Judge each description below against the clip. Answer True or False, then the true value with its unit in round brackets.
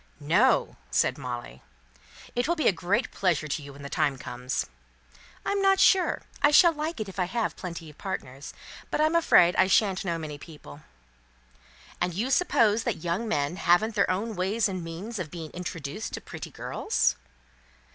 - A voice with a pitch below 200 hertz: True (185 Hz)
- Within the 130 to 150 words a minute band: False (180 wpm)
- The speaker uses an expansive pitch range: True (6.4 semitones)